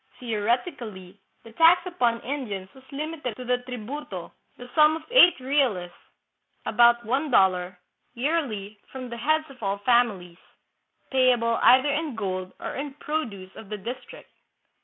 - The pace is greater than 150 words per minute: No, average, 145 wpm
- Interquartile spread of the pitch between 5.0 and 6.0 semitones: Yes, wide, 5.6 semitones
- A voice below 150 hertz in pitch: No, high, 245 Hz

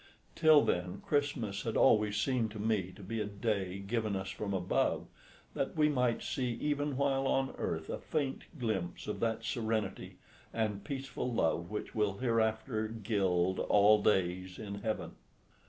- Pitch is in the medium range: No, low, 110 Hz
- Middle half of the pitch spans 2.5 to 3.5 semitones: No, average, 4.1 semitones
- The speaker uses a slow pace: No, average, 155 wpm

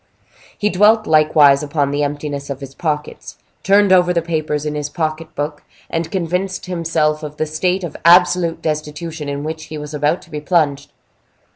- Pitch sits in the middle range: Yes, medium, 155 Hz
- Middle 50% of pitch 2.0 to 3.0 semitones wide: Yes, narrow, 2.6 semitones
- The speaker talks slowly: No, average, 175 wpm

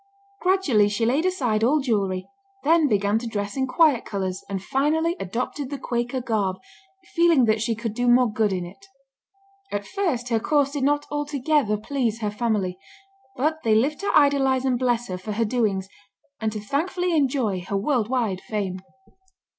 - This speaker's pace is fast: No, average, 170 wpm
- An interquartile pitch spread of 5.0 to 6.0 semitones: Yes, wide, 5.4 semitones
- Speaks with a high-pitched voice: Yes, high, 240 Hz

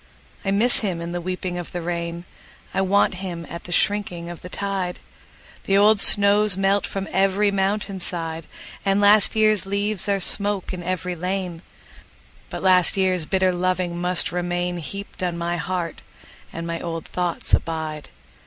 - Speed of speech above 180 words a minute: No, average, 150 wpm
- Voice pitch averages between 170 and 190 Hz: Yes, medium, 185 Hz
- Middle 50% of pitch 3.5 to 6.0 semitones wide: No, narrow, 2.4 semitones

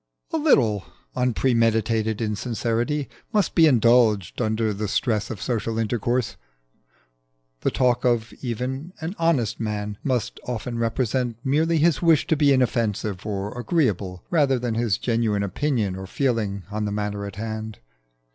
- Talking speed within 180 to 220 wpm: No, average, 140 wpm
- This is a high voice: No, low, 115 Hz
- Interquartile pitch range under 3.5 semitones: No, average, 3.8 semitones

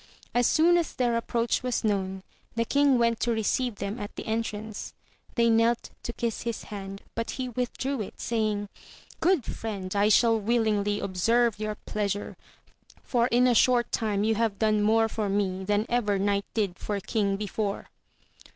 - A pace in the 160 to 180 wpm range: Yes, average, 170 wpm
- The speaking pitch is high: Yes, high, 220 Hz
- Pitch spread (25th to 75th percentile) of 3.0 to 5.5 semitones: No, narrow, 2.6 semitones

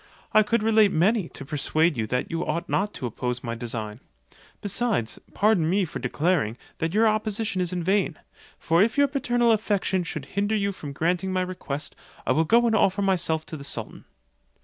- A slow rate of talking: No, average, 190 wpm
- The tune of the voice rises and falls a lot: Yes, wide, 5.8 semitones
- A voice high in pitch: No, medium, 180 Hz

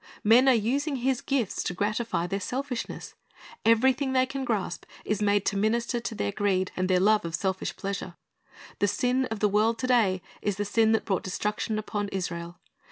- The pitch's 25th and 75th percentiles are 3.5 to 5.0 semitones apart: Yes, average, 3.9 semitones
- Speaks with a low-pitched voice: No, high, 215 Hz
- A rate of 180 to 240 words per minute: Yes, average, 190 wpm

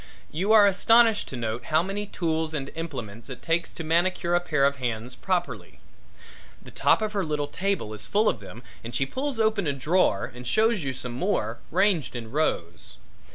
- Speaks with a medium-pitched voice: Yes, medium, 160 Hz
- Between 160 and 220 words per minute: Yes, average, 195 wpm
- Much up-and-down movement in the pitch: Yes, wide, 7.8 semitones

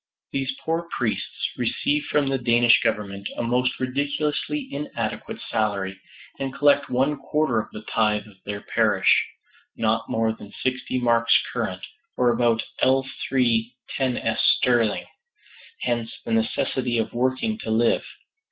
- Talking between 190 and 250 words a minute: No, slow, 135 wpm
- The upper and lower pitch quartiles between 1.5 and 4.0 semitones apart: Yes, average, 3.2 semitones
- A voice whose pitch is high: No, low, 120 Hz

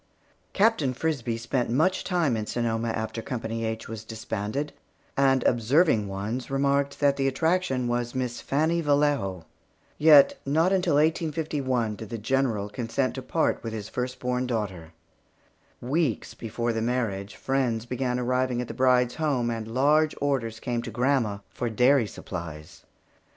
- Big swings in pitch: No, average, 3.8 semitones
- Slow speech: No, average, 150 wpm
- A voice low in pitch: Yes, low, 125 Hz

